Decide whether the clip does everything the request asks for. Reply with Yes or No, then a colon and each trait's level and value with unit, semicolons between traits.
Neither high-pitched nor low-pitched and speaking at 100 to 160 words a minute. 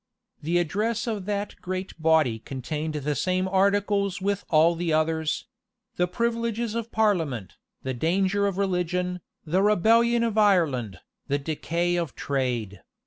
Yes: medium, 180 Hz; average, 140 wpm